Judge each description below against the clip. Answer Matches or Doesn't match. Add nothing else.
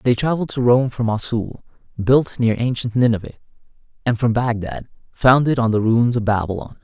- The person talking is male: Matches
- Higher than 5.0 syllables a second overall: Matches